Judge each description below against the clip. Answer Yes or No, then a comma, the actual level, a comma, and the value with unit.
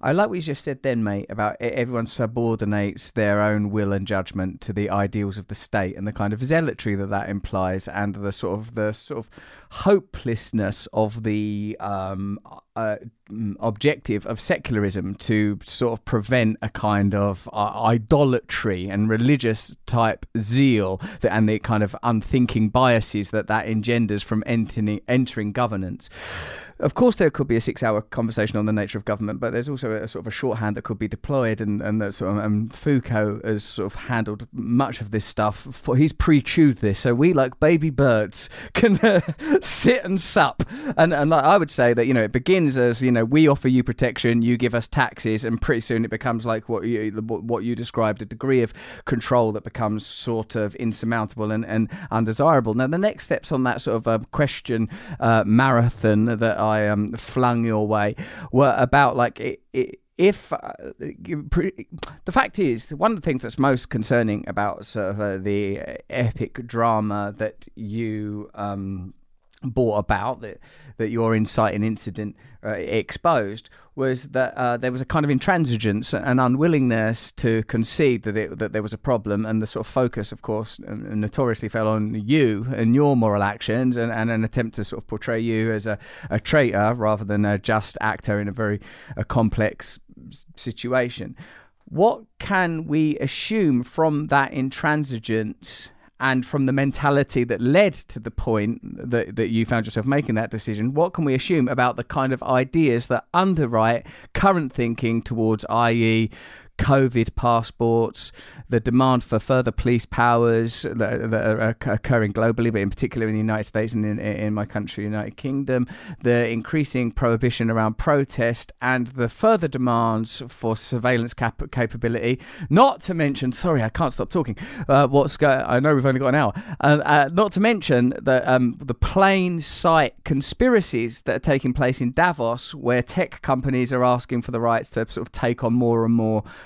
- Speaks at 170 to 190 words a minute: Yes, average, 185 wpm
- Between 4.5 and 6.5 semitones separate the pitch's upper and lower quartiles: No, average, 3.3 semitones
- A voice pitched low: Yes, low, 115 Hz